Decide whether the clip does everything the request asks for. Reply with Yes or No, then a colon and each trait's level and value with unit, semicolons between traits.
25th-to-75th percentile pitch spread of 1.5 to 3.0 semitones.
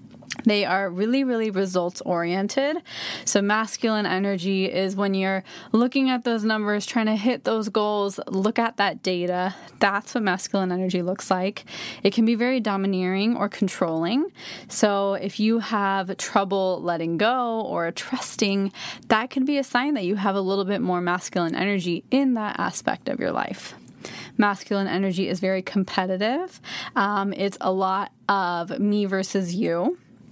Yes: average, 2.7 semitones